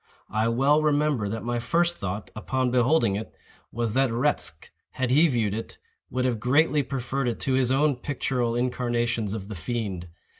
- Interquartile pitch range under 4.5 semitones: Yes, average, 3.2 semitones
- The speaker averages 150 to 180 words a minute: Yes, average, 175 wpm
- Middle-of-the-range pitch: No, low, 125 Hz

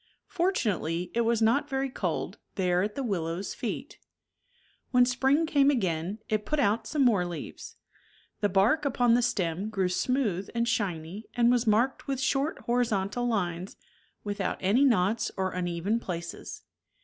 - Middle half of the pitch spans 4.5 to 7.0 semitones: Yes, average, 5.1 semitones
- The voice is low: No, high, 220 Hz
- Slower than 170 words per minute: Yes, average, 150 wpm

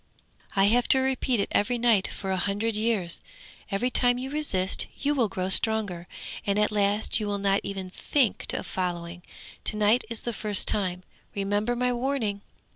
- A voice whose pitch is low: No, high, 210 Hz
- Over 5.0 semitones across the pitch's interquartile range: No, average, 3.7 semitones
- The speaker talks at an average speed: Yes, average, 180 wpm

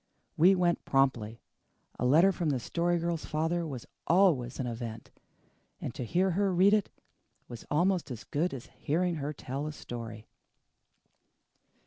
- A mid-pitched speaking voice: Yes, medium, 155 Hz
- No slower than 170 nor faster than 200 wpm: No, average, 150 wpm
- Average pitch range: No, wide, 5.8 semitones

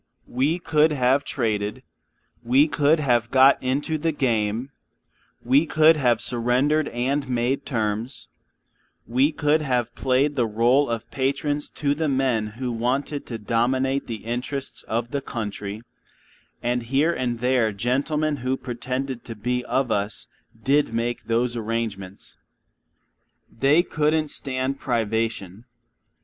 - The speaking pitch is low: Yes, low, 125 Hz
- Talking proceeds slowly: Yes, slow, 130 wpm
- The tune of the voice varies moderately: Yes, average, 3.4 semitones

